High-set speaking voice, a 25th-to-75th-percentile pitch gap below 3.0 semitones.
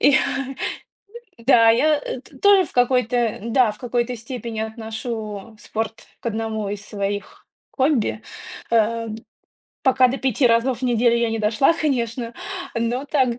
Yes: high, 235 Hz; narrow, 2.6 semitones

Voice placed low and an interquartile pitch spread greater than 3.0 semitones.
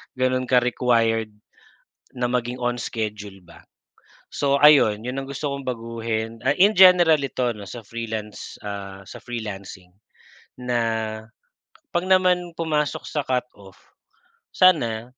Yes: low, 120 Hz; average, 4.1 semitones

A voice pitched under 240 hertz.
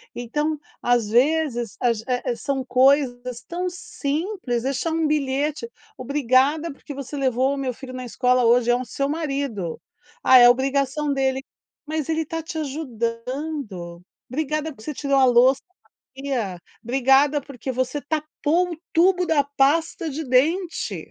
No: very high, 275 Hz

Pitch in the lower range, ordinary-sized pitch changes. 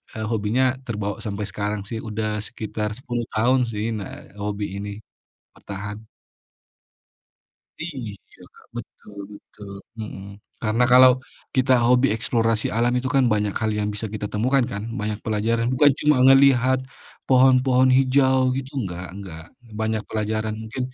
Yes: low, 110 Hz; average, 3.5 semitones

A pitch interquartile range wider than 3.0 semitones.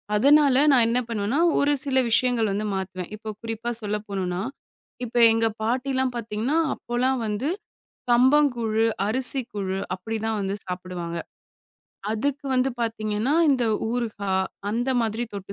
Yes: average, 3.7 semitones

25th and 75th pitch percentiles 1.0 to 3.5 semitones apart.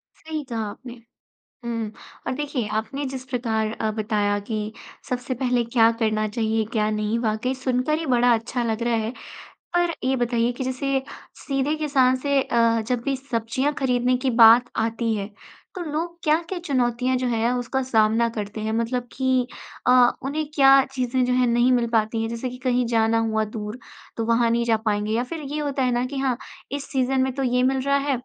Yes: average, 2.8 semitones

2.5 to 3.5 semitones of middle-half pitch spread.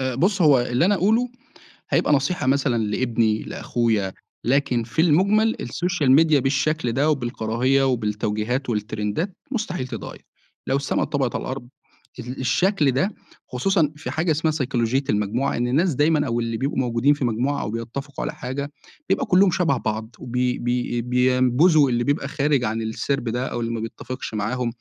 No: average, 4.0 semitones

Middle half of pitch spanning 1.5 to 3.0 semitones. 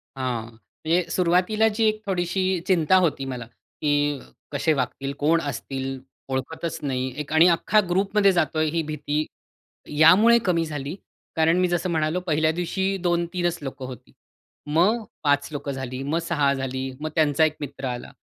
No: average, 4.0 semitones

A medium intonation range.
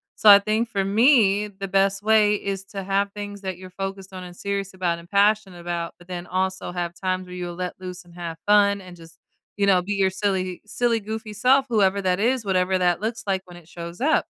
No: narrow, 2.3 semitones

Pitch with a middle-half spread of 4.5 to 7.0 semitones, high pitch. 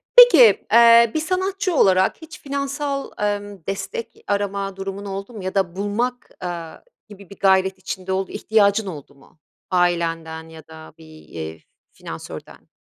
Yes: average, 4.8 semitones; high, 195 Hz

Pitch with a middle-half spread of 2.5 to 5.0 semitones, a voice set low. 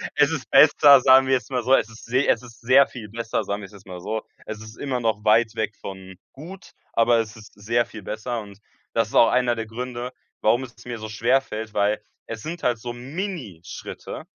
Yes: average, 2.9 semitones; low, 115 Hz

